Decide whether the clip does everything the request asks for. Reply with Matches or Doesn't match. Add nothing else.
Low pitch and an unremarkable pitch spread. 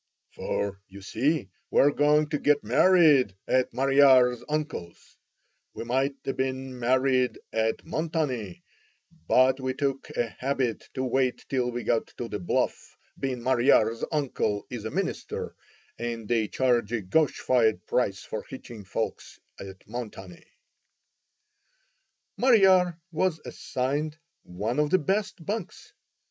Matches